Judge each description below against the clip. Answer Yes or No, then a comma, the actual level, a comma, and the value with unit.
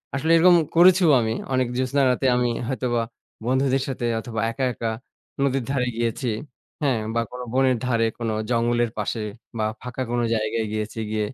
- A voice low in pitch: Yes, low, 125 Hz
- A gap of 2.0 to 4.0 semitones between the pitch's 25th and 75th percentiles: Yes, narrow, 2.4 semitones